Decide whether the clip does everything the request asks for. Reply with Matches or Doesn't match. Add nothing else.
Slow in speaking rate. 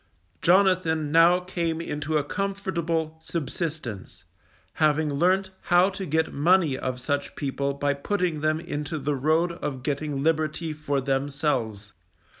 Matches